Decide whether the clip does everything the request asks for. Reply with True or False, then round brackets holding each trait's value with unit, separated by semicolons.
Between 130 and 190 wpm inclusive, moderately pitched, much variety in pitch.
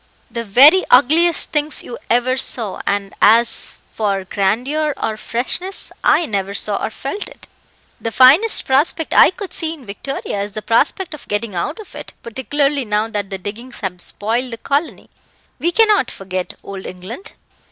False (165 wpm; 240 Hz; 6.5 semitones)